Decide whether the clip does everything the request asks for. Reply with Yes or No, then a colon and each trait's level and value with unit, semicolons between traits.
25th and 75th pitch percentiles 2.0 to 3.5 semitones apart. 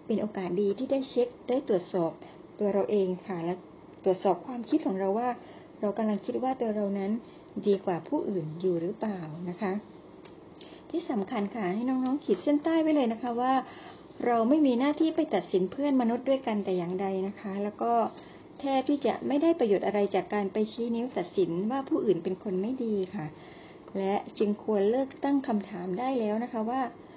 No: average, 5.2 semitones